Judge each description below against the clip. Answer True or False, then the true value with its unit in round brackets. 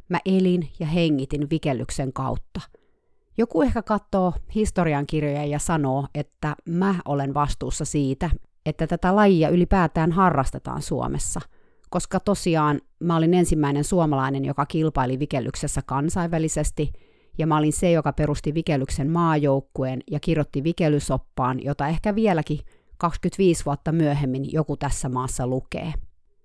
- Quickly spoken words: False (125 wpm)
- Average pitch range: True (3.7 semitones)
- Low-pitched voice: False (155 Hz)